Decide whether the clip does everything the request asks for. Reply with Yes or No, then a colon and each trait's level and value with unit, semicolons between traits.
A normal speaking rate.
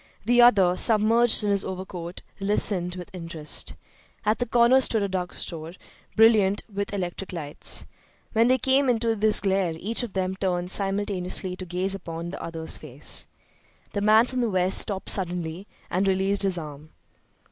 Yes: average, 165 wpm